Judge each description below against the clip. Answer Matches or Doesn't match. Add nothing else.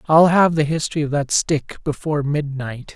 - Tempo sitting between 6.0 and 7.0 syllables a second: Doesn't match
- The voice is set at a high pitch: Doesn't match